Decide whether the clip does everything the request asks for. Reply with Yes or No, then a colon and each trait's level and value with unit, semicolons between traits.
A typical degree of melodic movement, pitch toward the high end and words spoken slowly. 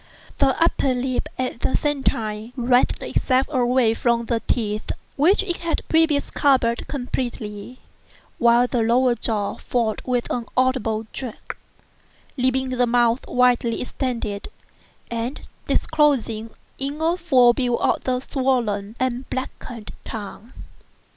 No: narrow, 2.2 semitones; high, 245 Hz; slow, 120 wpm